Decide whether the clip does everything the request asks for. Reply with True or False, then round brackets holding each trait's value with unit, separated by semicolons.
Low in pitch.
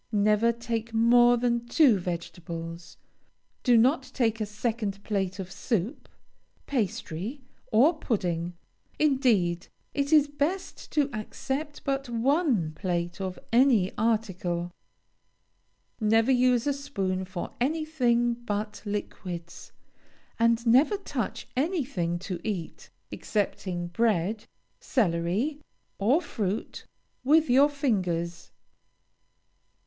False (225 Hz)